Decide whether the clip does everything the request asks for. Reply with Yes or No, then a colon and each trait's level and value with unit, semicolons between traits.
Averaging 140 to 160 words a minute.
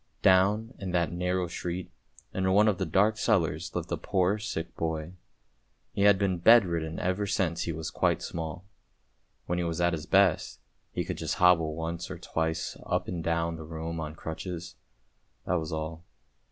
No: average, 185 wpm